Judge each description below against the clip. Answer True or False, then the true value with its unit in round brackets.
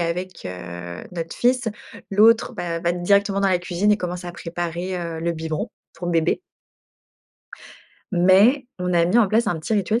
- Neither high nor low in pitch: True (180 Hz)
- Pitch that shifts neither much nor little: True (3.1 semitones)